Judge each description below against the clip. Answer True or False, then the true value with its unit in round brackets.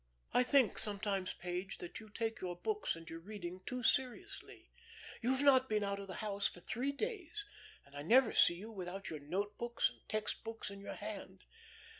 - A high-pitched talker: True (210 Hz)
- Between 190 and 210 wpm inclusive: True (195 wpm)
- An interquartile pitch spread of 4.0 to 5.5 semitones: True (4.9 semitones)